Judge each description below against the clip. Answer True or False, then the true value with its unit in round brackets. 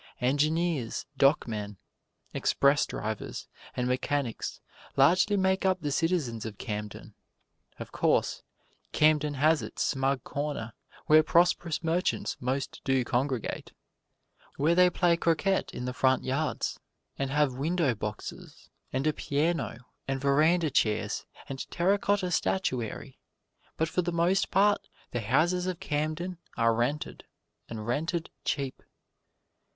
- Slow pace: True (125 wpm)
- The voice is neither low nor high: True (145 Hz)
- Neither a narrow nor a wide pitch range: True (5.0 semitones)